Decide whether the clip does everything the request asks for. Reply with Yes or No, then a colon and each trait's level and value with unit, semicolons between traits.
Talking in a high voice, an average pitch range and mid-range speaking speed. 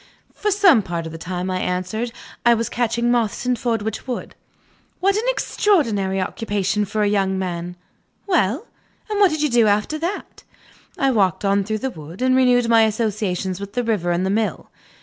Yes: high, 220 Hz; average, 4.7 semitones; average, 190 wpm